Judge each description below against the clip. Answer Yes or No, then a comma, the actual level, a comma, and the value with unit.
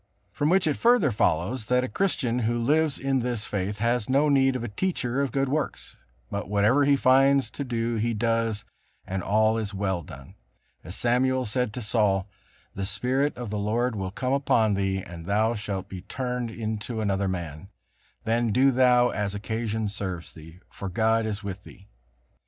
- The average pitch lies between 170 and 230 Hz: No, low, 115 Hz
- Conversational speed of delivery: Yes, average, 185 wpm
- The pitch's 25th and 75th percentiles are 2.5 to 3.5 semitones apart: No, average, 4.1 semitones